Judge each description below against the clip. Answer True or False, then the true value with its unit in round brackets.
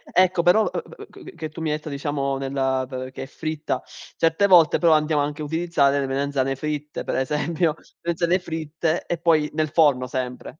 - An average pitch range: True (3.0 semitones)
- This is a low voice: False (150 Hz)